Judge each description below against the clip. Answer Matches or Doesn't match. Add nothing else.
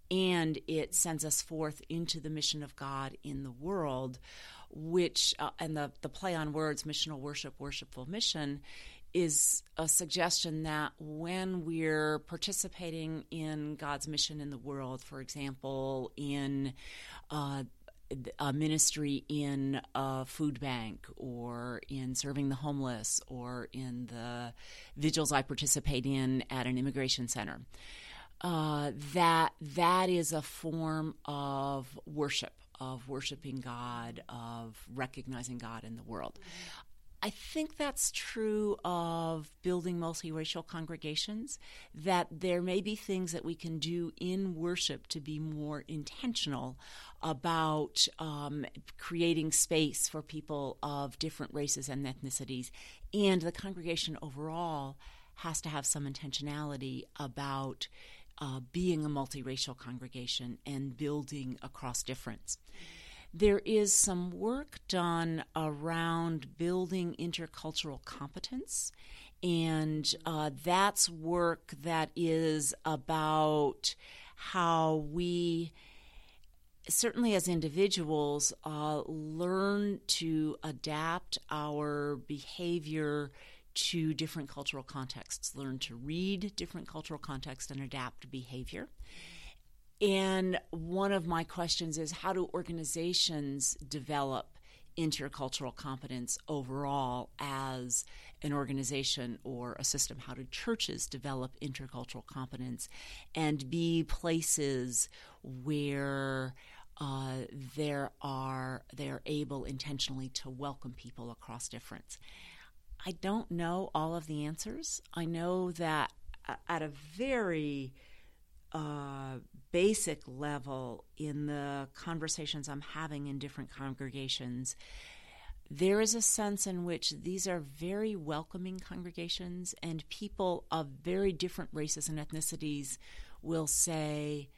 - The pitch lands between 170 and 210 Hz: Doesn't match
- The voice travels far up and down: Doesn't match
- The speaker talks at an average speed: Doesn't match